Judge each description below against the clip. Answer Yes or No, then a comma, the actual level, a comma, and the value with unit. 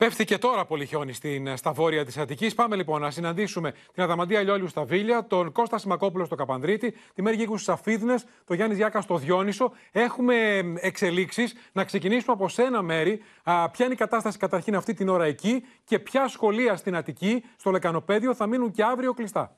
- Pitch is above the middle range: Yes, high, 200 Hz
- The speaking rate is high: Yes, fast, 190 wpm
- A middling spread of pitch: Yes, average, 4.5 semitones